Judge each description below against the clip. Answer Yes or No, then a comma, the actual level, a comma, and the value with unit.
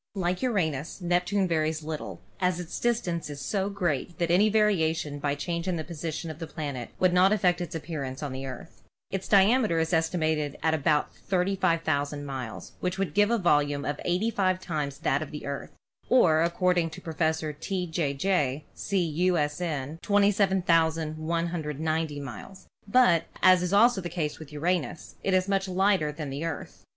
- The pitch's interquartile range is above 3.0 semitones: Yes, average, 3.6 semitones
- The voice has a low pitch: No, medium, 165 Hz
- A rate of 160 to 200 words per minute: Yes, average, 170 wpm